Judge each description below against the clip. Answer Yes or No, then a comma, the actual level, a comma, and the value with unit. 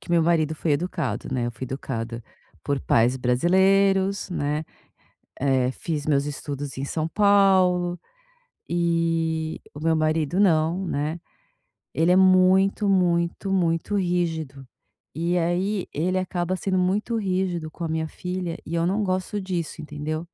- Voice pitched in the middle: Yes, medium, 170 Hz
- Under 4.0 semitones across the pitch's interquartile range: Yes, average, 3.2 semitones